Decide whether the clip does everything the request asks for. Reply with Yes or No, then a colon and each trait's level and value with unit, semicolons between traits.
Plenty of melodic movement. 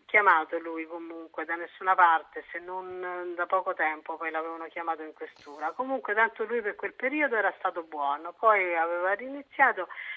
No: average, 2.7 semitones